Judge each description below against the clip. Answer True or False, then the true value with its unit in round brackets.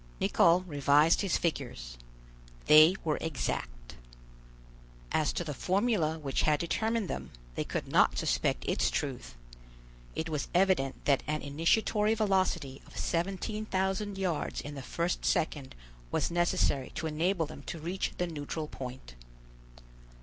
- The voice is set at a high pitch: False (160 Hz)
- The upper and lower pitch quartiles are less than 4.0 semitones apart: False (4.6 semitones)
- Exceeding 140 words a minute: False (135 wpm)